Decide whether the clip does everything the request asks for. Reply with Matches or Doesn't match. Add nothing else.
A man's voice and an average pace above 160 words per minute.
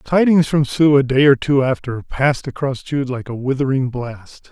Matches